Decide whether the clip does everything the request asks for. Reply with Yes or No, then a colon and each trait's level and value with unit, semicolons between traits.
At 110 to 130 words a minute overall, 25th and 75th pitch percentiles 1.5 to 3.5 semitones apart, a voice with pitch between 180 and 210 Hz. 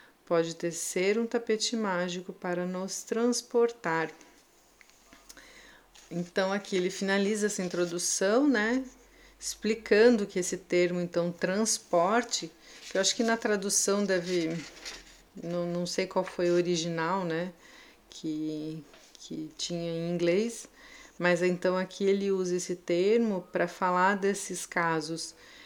Yes: average, 125 wpm; average, 2.8 semitones; medium, 185 Hz